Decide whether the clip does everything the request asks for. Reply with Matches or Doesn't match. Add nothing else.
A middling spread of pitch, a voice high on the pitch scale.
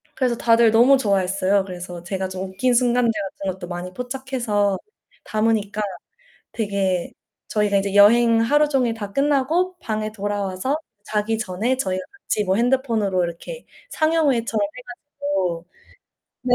Matches